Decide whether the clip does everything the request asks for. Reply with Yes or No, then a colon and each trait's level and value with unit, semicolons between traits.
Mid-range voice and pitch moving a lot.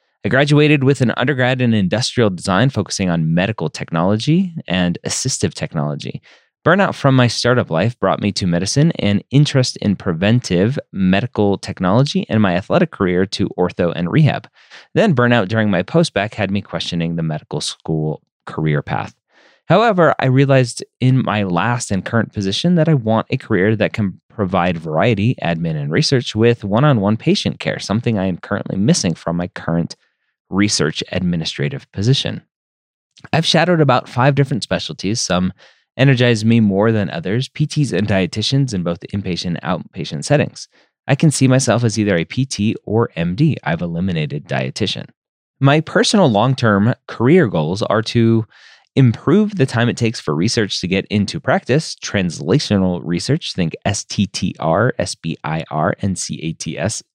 No: low, 110 Hz; wide, 6.2 semitones